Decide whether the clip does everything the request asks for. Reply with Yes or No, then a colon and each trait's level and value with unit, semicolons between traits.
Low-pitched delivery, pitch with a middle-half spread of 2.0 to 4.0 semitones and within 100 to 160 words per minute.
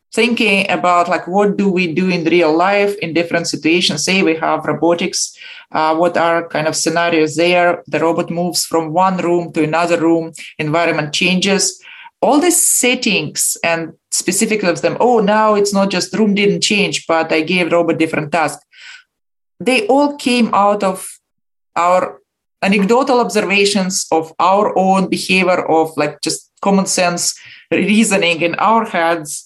No: medium, 180 Hz; average, 3.4 semitones; average, 155 wpm